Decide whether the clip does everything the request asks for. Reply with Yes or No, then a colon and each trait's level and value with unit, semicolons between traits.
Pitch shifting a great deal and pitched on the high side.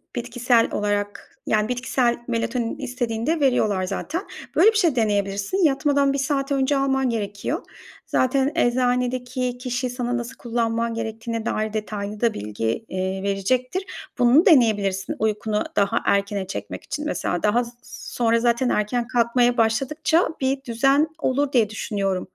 No: average, 3.7 semitones; high, 240 Hz